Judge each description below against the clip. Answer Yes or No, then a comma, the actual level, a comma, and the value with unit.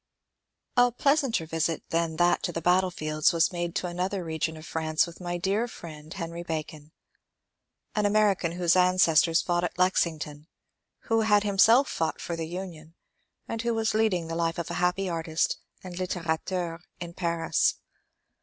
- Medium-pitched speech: Yes, medium, 175 Hz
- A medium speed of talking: Yes, average, 165 wpm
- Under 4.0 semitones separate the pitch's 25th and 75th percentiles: Yes, narrow, 2.6 semitones